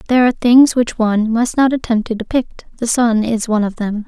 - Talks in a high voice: Yes, high, 230 Hz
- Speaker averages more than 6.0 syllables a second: No, 5.9 syllables/s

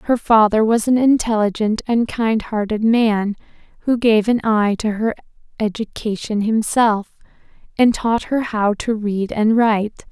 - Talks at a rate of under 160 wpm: Yes, average, 150 wpm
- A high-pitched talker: Yes, high, 220 Hz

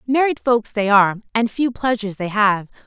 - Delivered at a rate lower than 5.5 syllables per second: No, 5.6 syllables/s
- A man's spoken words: No, female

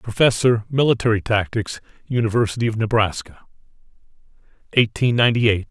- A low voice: Yes, low, 115 Hz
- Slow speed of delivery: Yes, slow, 95 wpm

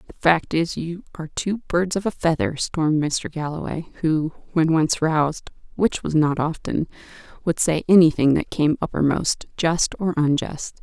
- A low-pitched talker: No, medium, 160 Hz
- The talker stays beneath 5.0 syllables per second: Yes, 4.6 syllables/s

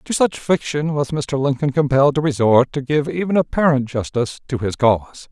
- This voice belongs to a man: Yes, male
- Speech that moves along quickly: No, average, 190 wpm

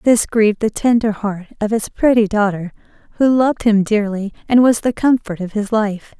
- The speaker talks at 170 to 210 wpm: Yes, average, 195 wpm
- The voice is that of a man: No, female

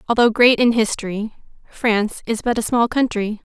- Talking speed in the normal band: Yes, average, 170 wpm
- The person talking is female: Yes, female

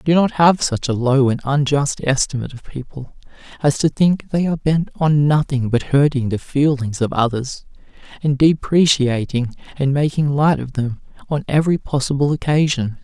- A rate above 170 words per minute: No, average, 165 wpm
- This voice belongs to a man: Yes, male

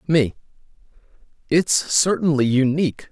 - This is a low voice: No, medium, 145 Hz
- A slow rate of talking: Yes, slow, 75 wpm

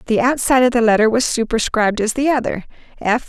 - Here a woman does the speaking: Yes, female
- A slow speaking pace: No, average, 200 wpm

